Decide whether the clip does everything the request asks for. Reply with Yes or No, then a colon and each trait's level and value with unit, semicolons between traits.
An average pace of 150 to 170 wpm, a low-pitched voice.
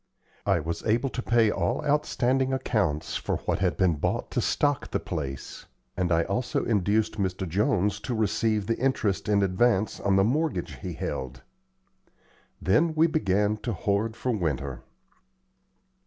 Yes: average, 155 wpm; low, 105 Hz